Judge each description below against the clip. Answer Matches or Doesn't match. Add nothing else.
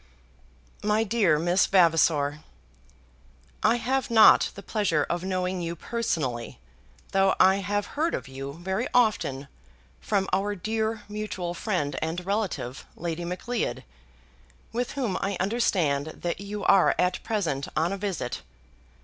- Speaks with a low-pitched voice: Doesn't match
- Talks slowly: Matches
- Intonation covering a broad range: Doesn't match